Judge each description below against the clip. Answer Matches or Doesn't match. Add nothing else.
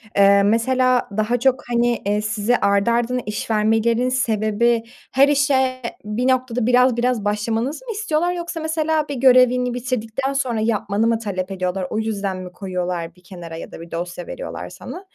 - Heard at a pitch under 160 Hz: Doesn't match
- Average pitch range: Matches